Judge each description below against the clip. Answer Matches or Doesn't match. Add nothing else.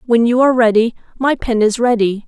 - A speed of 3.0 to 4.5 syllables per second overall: Doesn't match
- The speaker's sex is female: Matches